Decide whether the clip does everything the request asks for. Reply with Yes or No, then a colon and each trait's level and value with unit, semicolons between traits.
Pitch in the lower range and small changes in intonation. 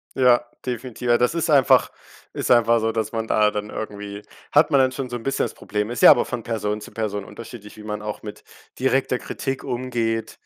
No: low, 115 Hz; average, 3.0 semitones